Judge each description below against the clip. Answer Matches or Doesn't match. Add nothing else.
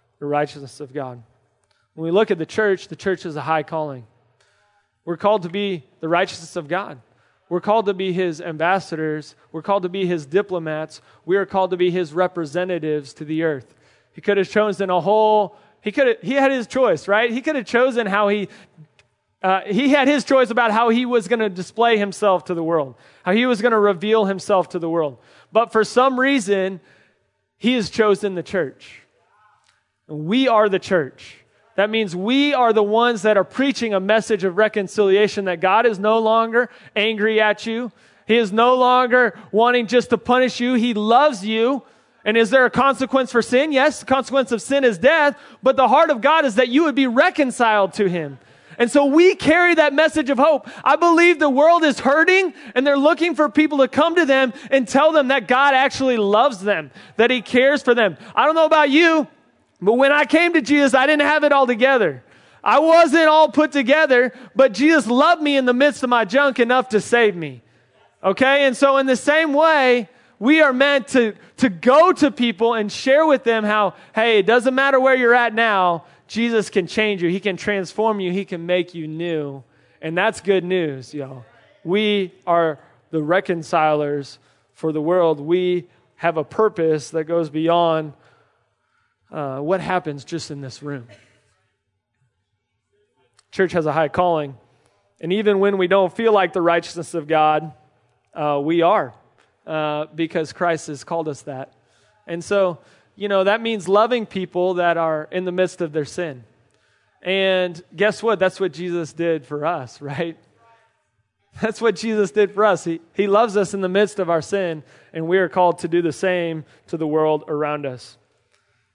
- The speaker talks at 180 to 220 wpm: Matches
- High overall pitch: Matches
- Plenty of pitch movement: Matches